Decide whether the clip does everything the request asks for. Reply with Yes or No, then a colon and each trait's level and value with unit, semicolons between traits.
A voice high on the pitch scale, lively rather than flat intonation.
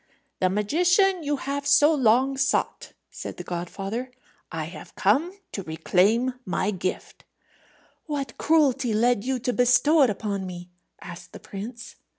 Yes: high, 245 Hz; wide, 6.4 semitones